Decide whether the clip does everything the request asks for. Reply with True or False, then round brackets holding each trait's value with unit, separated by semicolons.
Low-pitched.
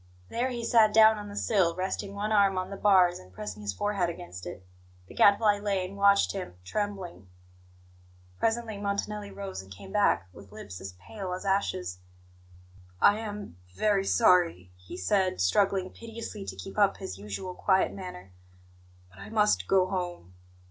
False (190 Hz)